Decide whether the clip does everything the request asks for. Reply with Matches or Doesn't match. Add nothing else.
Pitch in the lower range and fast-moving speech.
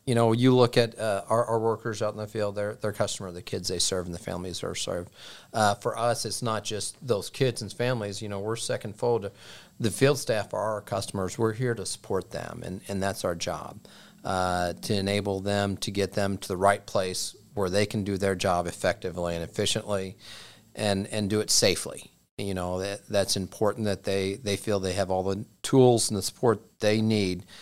Matches